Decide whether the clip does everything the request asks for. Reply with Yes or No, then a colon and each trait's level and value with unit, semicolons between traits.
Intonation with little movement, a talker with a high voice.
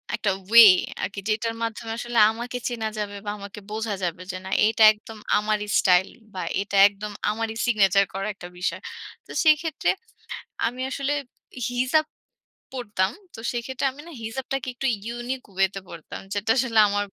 No: average, 3.2 semitones; high, 220 Hz